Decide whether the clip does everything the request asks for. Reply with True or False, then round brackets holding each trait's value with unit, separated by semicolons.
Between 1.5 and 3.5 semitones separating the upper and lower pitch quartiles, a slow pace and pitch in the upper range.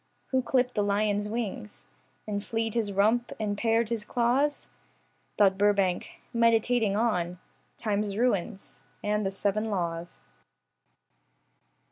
True (2.6 semitones; 115 wpm; 210 Hz)